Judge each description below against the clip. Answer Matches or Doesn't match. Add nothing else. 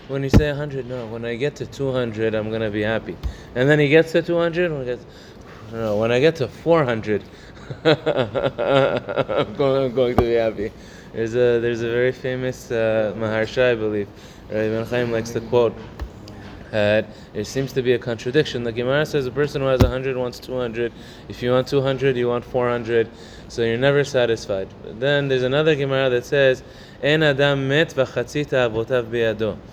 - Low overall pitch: Matches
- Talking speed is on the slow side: Doesn't match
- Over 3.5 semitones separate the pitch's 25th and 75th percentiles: Doesn't match